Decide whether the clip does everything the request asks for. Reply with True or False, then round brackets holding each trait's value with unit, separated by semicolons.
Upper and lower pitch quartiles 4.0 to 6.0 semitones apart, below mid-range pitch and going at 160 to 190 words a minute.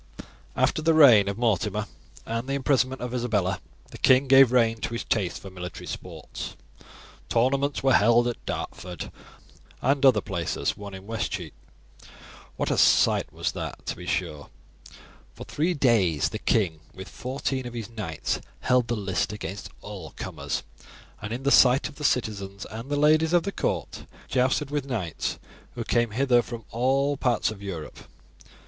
True (5.0 semitones; 120 Hz; 165 wpm)